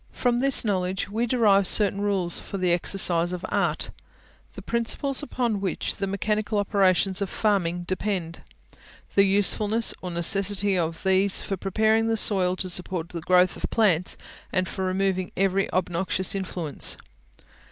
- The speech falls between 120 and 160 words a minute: Yes, average, 150 wpm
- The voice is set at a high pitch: Yes, high, 195 Hz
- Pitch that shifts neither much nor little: No, narrow, 2.2 semitones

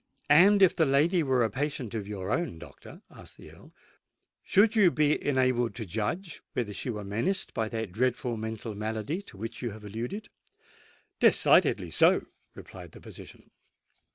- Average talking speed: Yes, average, 165 wpm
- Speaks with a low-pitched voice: Yes, low, 120 Hz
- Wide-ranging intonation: Yes, wide, 6.5 semitones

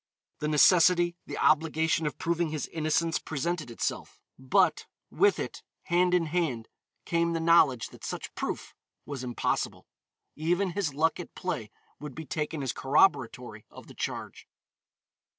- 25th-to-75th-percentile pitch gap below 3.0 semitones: No, average, 3.3 semitones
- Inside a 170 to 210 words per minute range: No, average, 145 wpm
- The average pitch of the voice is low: No, medium, 160 Hz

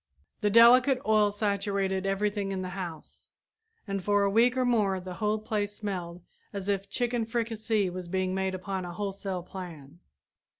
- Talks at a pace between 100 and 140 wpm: No, average, 165 wpm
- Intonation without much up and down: Yes, narrow, 2.3 semitones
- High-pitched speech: Yes, high, 200 Hz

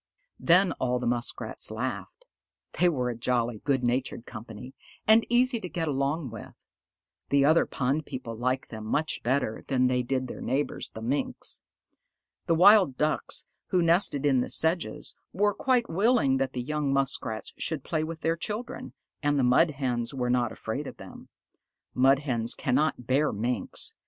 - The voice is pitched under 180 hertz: Yes, low, 135 Hz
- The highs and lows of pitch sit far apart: No, average, 4.6 semitones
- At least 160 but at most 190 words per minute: Yes, average, 165 wpm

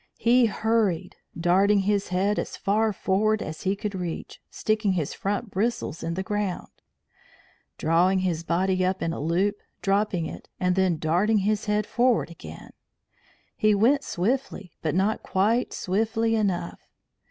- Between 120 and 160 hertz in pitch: No, high, 195 Hz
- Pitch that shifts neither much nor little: Yes, average, 3.1 semitones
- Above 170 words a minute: No, average, 150 wpm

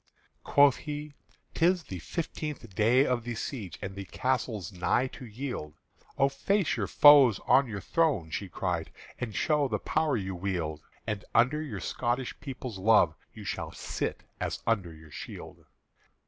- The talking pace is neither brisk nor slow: Yes, average, 160 wpm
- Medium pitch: No, low, 120 Hz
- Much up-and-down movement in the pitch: Yes, wide, 6.6 semitones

